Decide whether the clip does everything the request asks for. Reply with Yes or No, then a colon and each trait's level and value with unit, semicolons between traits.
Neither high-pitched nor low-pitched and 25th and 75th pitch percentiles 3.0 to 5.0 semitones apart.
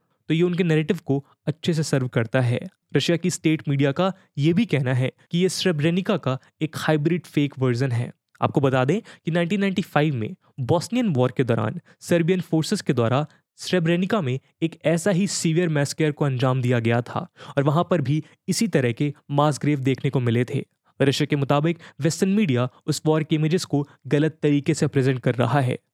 Yes: medium, 155 Hz; average, 4.0 semitones